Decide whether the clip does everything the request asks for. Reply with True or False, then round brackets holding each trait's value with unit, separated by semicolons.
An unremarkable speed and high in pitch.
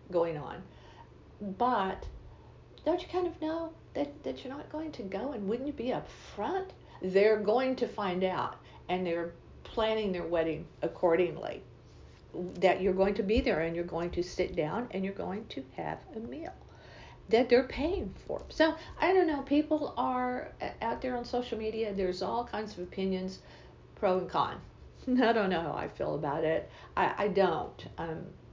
True (180 wpm; 215 Hz)